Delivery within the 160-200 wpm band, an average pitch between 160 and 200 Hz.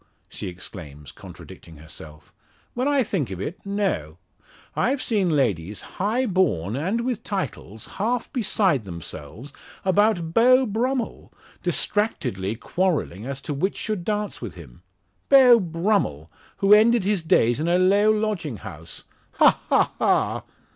No: slow, 135 wpm; medium, 185 Hz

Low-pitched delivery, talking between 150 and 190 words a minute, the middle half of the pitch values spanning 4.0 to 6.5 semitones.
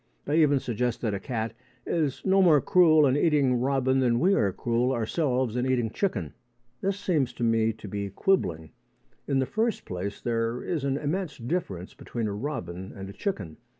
Yes: low, 125 Hz; average, 185 wpm; wide, 5.5 semitones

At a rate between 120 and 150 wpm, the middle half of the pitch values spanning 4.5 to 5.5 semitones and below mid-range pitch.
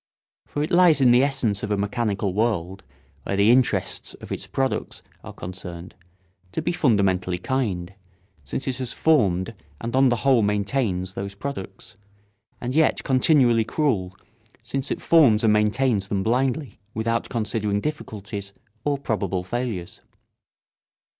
Yes: average, 140 wpm; average, 5.1 semitones; low, 110 Hz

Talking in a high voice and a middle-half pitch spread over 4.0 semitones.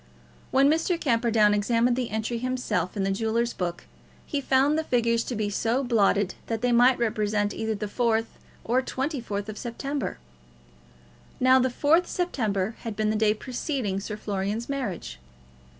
No: high, 230 Hz; average, 3.6 semitones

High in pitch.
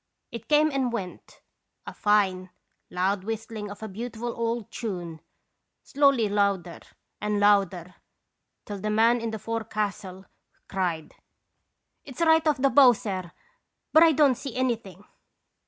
Yes: high, 215 Hz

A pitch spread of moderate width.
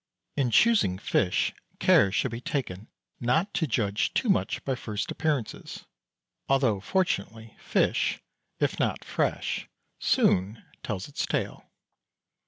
No: wide, 6.1 semitones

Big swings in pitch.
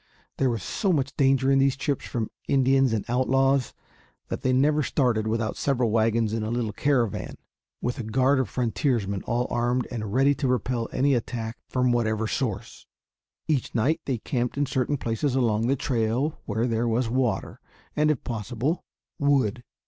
No: average, 3.0 semitones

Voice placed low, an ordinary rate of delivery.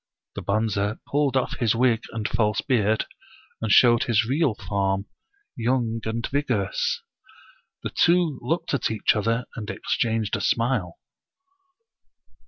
No: low, 115 Hz; slow, 130 wpm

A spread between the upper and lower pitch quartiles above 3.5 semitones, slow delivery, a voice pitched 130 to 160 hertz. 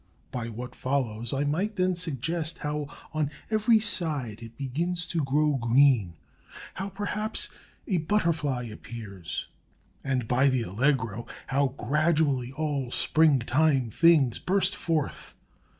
Yes: average, 5.1 semitones; slow, 120 wpm; medium, 140 Hz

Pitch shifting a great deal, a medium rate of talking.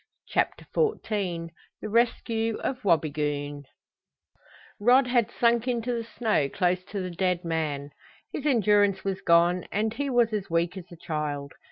Yes: wide, 5.7 semitones; average, 150 wpm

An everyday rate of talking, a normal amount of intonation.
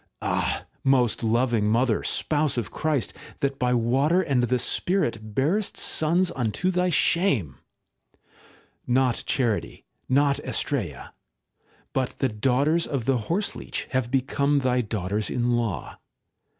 No: slow, 125 wpm; average, 3.8 semitones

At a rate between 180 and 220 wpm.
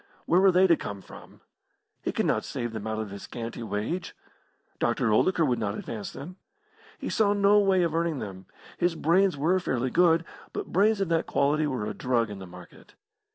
Yes: average, 200 wpm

